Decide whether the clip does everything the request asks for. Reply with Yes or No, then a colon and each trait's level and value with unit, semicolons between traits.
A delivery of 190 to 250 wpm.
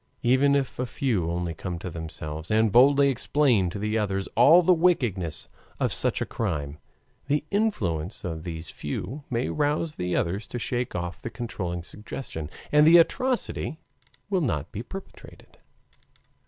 No: average, 155 wpm